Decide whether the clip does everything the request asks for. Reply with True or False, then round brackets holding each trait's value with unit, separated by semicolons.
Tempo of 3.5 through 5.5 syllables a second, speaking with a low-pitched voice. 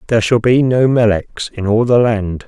True (4.9 syllables/s; 115 Hz)